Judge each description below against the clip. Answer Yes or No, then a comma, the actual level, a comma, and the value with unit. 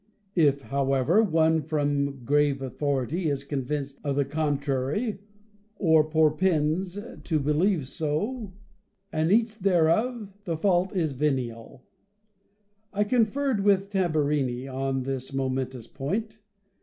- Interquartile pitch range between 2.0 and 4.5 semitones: No, wide, 5.6 semitones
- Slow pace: Yes, slow, 120 wpm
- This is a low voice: No, medium, 150 Hz